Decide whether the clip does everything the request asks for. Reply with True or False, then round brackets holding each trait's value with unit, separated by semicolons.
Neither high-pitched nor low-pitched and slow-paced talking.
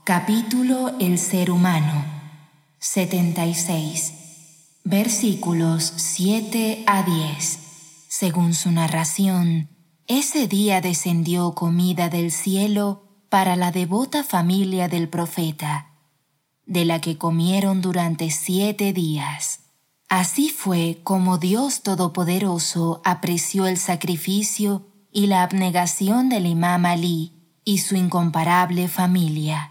True (180 Hz; 100 wpm)